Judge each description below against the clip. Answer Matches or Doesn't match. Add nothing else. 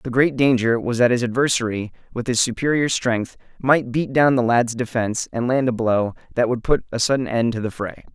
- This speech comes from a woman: Doesn't match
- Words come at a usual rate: Doesn't match